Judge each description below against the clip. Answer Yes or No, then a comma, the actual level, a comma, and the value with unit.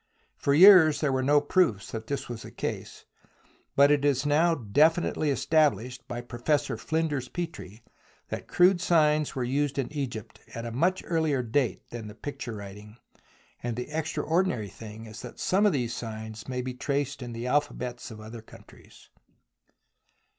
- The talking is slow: No, average, 165 wpm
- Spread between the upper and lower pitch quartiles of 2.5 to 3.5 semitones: No, average, 4.7 semitones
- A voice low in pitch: Yes, low, 130 Hz